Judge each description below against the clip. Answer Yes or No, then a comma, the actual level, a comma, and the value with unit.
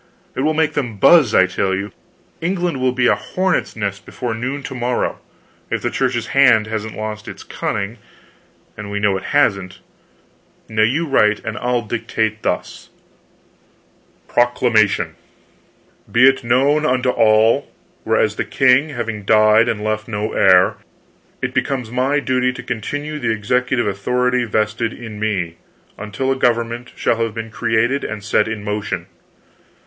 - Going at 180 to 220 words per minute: No, average, 155 wpm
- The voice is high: No, low, 115 Hz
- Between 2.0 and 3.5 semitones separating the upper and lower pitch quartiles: Yes, average, 3.1 semitones